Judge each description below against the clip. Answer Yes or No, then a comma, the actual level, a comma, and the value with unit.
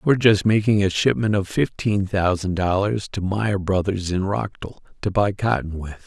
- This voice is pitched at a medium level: No, low, 100 Hz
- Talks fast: No, average, 180 wpm